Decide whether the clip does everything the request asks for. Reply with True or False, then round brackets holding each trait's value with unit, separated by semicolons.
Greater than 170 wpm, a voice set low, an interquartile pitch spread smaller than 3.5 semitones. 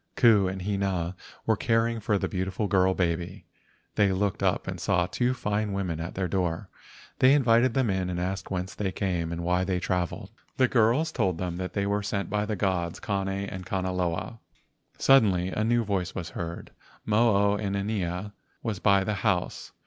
True (180 wpm; 95 Hz; 2.7 semitones)